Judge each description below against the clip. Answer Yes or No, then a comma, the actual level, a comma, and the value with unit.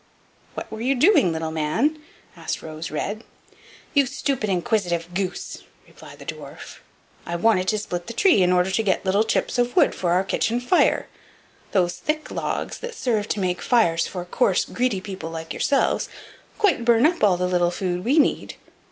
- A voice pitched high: Yes, high, 200 Hz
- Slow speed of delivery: No, average, 180 wpm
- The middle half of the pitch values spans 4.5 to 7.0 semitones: Yes, wide, 5.6 semitones